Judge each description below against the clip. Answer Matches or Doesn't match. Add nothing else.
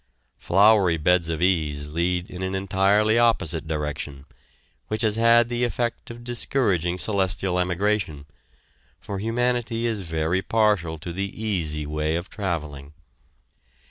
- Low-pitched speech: Matches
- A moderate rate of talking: Doesn't match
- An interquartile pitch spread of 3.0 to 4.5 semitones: Doesn't match